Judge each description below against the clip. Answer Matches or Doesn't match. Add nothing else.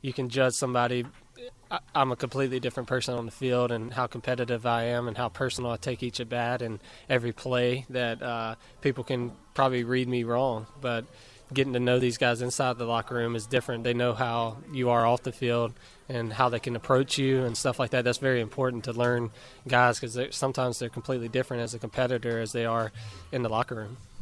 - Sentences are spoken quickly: Matches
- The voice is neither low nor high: Doesn't match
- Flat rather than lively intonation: Matches